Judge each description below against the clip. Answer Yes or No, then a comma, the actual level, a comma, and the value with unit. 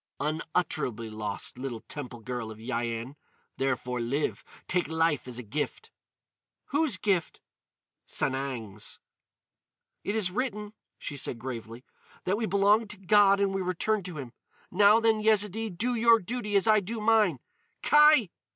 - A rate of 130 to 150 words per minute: Yes, average, 140 wpm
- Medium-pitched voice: Yes, medium, 180 Hz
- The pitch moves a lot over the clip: Yes, wide, 8.9 semitones